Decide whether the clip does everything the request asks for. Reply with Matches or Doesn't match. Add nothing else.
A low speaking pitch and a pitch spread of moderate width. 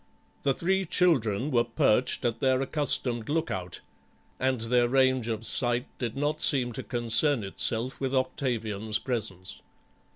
Matches